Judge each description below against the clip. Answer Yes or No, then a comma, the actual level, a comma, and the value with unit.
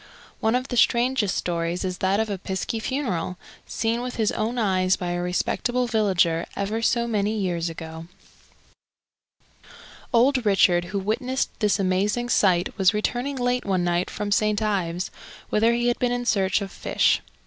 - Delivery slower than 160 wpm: No, average, 165 wpm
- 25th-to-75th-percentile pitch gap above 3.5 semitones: Yes, average, 4.4 semitones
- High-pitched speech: Yes, high, 210 Hz